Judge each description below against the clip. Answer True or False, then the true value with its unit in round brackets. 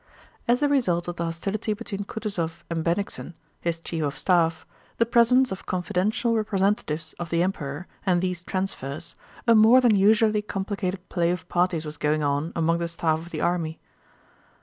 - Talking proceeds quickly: False (170 wpm)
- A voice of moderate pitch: True (180 Hz)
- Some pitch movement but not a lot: True (4.1 semitones)